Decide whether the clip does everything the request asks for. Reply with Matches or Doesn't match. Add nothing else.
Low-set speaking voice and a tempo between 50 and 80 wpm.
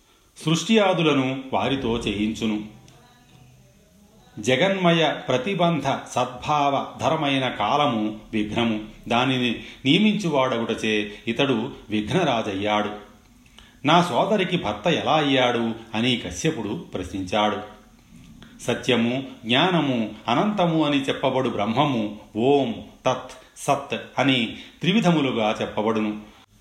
Matches